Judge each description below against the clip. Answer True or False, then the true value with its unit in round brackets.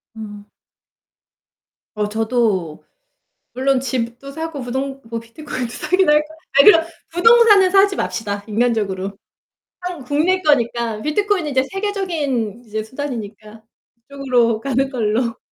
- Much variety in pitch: True (5.7 semitones)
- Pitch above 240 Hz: True (255 Hz)